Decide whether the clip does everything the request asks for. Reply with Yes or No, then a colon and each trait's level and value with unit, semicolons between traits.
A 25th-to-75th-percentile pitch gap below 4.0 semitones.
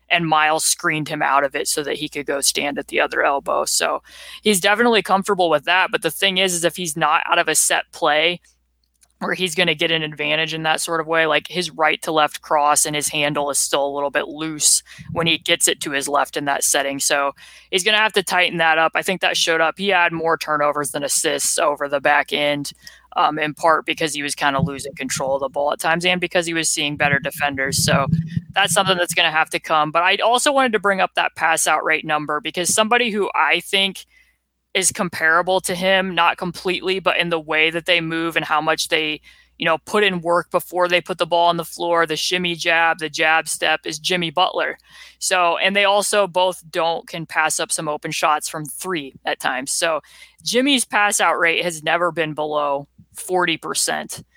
Yes: average, 2.9 semitones